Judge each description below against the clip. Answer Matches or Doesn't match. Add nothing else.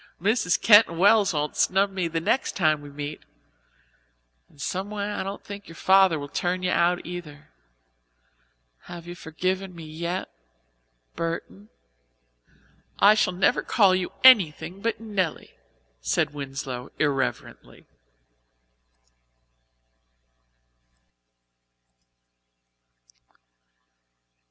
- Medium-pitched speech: Matches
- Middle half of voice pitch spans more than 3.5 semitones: Matches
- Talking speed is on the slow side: Matches